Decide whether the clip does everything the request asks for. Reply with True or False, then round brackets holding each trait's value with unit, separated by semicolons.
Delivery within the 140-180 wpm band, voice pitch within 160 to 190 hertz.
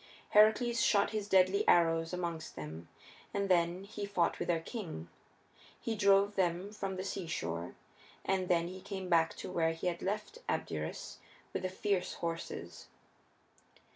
True (150 wpm; 185 Hz)